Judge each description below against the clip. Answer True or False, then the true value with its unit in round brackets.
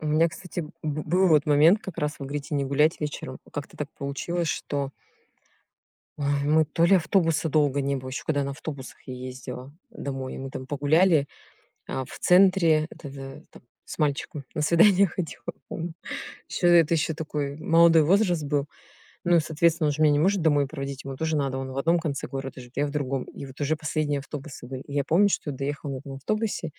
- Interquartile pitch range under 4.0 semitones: True (2.9 semitones)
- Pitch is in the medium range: True (150 Hz)